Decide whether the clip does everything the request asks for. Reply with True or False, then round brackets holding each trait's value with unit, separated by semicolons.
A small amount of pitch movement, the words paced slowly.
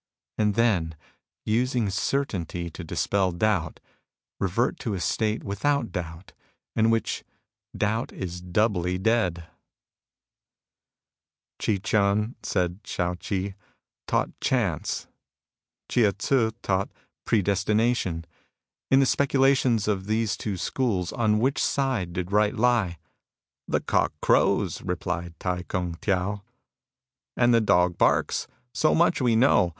False (4.2 semitones; 125 wpm)